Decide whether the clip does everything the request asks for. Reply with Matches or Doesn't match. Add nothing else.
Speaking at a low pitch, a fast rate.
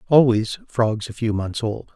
Doesn't match